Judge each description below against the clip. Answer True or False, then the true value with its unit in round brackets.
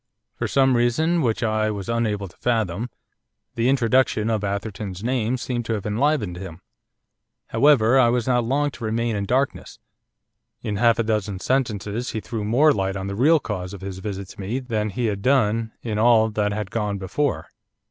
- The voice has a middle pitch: False (110 Hz)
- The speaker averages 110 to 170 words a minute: False (190 wpm)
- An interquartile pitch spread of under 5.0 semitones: True (3.3 semitones)